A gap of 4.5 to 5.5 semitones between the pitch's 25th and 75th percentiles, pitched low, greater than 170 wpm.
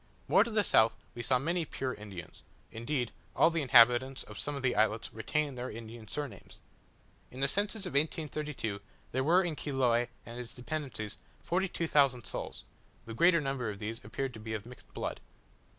Yes: average, 4.8 semitones; low, 130 Hz; average, 185 wpm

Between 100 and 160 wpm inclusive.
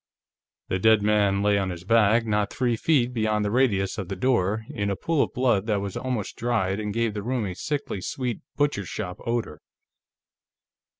No: average, 185 wpm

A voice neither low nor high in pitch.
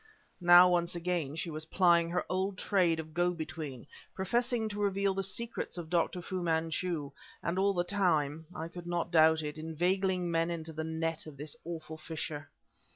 Yes: medium, 170 Hz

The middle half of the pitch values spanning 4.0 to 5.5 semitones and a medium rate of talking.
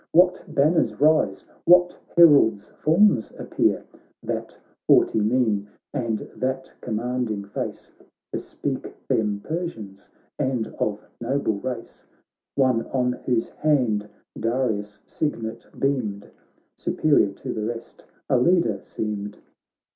No: average, 4.9 semitones; slow, 105 wpm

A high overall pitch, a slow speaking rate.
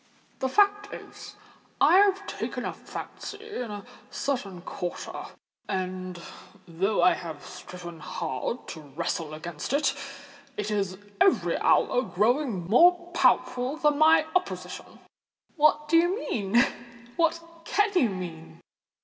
Yes: high, 245 Hz; slow, 125 wpm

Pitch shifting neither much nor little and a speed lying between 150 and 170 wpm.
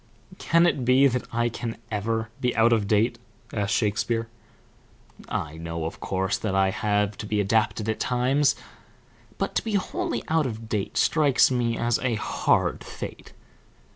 Yes: average, 3.5 semitones; average, 165 wpm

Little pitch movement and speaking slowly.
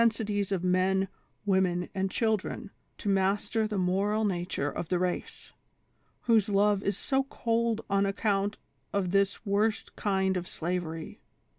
No: narrow, 2.2 semitones; average, 150 wpm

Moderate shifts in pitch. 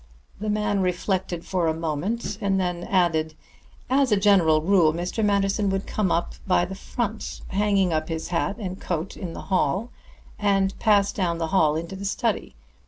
Yes: average, 3.1 semitones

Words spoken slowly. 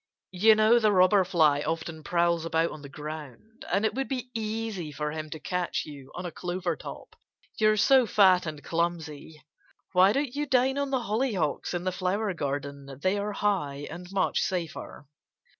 No: average, 180 wpm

